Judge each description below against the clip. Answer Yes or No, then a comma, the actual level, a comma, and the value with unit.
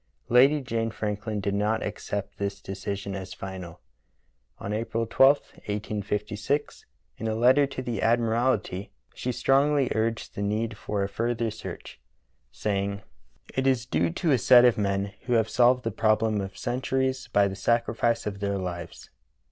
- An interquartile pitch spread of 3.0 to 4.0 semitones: Yes, average, 3.3 semitones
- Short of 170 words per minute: Yes, average, 155 wpm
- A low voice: Yes, low, 110 Hz